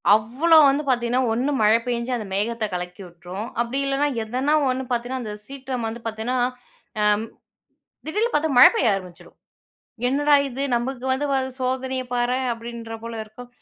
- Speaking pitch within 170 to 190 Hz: No, high, 245 Hz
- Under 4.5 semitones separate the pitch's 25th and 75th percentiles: Yes, average, 2.9 semitones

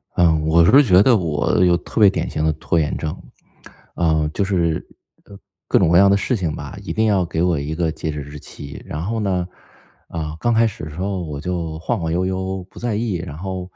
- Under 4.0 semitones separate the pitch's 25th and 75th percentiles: Yes, average, 3.6 semitones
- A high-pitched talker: No, very low, 90 Hz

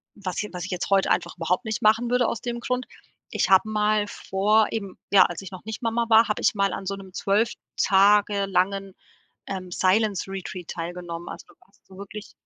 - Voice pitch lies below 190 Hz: No, high, 200 Hz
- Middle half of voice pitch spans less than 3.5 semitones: Yes, narrow, 2.5 semitones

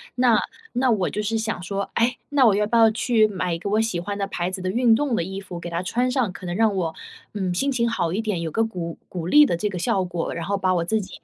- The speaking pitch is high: Yes, high, 200 Hz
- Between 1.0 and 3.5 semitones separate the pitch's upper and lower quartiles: No, average, 4.0 semitones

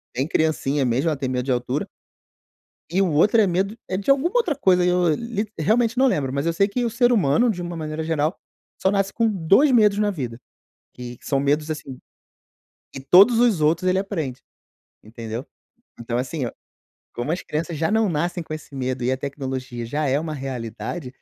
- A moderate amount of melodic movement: No, wide, 6.8 semitones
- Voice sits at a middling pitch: Yes, medium, 160 Hz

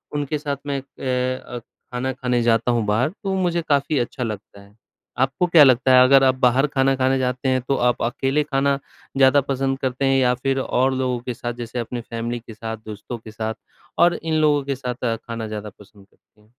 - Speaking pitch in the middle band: No, low, 130 Hz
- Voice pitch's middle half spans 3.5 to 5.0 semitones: No, narrow, 2.5 semitones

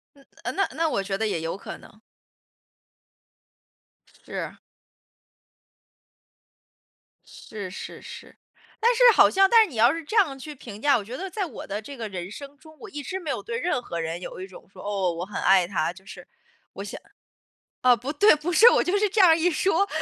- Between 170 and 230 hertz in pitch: No, very high, 275 Hz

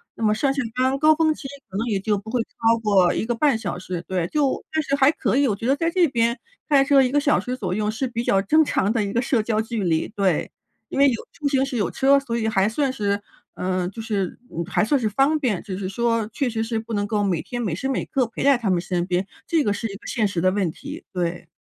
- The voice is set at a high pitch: Yes, high, 225 Hz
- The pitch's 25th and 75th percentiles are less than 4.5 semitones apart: No, wide, 5.4 semitones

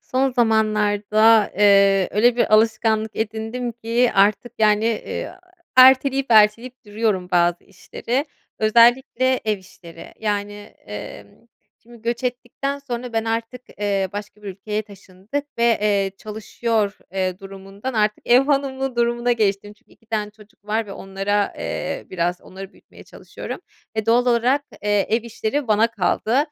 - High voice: Yes, high, 220 Hz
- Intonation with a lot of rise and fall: No, average, 2.8 semitones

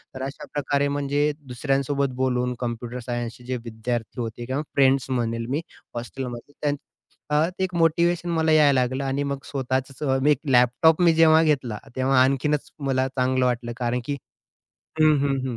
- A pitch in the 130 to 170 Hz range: Yes, low, 135 Hz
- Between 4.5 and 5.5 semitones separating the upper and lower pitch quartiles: No, average, 2.9 semitones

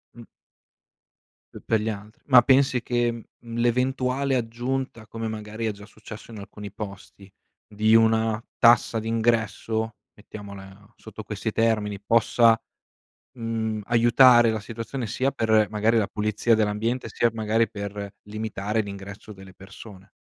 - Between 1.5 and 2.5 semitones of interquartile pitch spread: Yes, narrow, 1.9 semitones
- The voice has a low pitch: Yes, low, 110 Hz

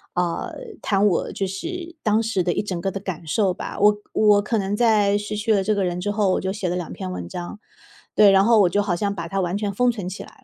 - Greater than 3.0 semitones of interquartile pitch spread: No, narrow, 2.5 semitones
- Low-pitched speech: No, high, 200 Hz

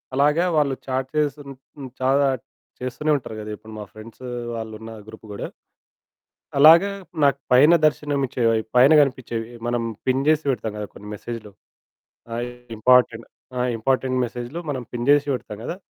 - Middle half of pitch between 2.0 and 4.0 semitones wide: Yes, average, 3.5 semitones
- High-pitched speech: No, low, 130 Hz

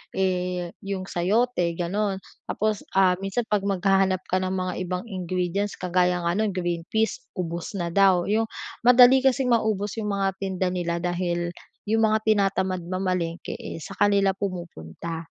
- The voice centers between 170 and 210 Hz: Yes, medium, 185 Hz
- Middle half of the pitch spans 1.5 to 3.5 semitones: Yes, narrow, 2.6 semitones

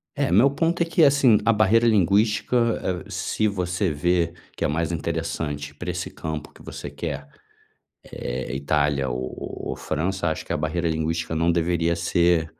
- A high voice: No, very low, 85 Hz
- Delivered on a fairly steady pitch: No, average, 4.0 semitones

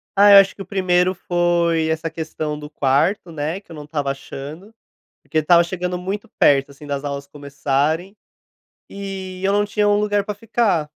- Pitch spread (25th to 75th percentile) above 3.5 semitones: Yes, average, 4.8 semitones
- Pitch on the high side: No, medium, 170 Hz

